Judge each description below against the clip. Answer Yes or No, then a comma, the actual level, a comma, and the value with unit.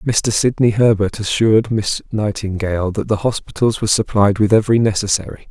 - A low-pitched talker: Yes, low, 105 Hz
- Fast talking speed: No, average, 155 wpm